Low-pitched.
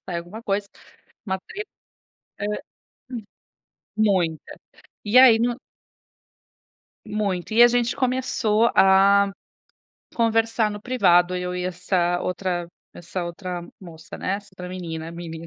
No: high, 195 Hz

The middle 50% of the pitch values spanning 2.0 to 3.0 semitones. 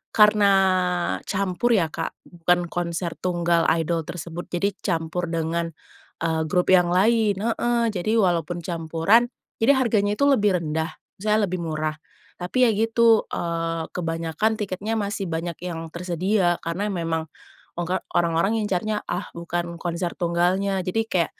No: average, 3.6 semitones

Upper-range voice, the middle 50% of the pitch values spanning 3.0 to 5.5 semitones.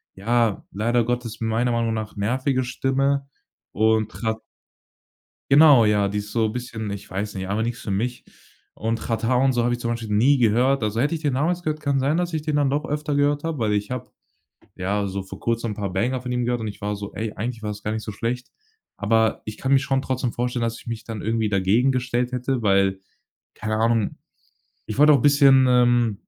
No: low, 115 Hz; average, 3.5 semitones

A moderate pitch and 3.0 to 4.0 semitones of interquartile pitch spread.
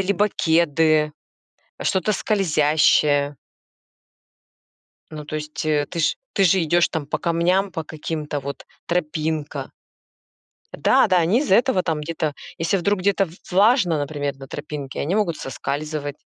Yes: medium, 160 Hz; average, 3.5 semitones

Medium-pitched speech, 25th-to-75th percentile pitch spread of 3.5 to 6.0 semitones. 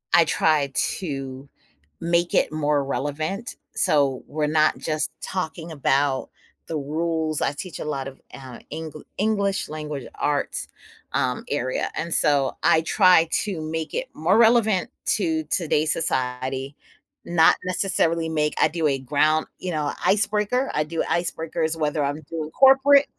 No: medium, 155 Hz; average, 3.0 semitones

